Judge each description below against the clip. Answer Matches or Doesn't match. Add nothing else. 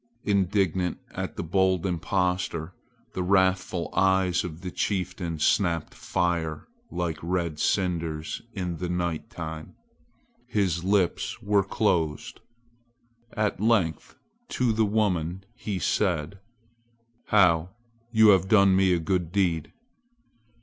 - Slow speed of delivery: Matches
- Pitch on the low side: Matches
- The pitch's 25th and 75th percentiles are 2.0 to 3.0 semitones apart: Matches